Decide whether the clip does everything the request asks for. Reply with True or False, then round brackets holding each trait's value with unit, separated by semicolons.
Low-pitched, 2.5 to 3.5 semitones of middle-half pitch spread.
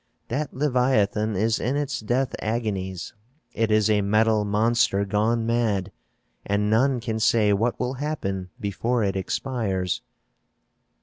True (110 Hz; 3.1 semitones)